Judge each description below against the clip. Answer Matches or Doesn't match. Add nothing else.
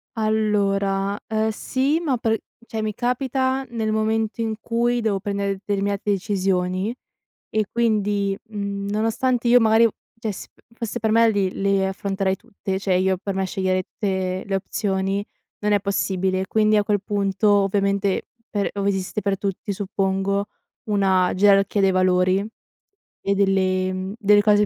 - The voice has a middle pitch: Doesn't match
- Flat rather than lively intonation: Matches